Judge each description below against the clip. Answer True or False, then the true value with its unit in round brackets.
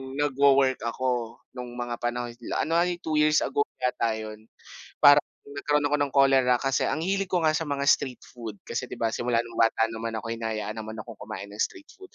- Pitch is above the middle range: False (125 Hz)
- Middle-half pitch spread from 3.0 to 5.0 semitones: True (4.2 semitones)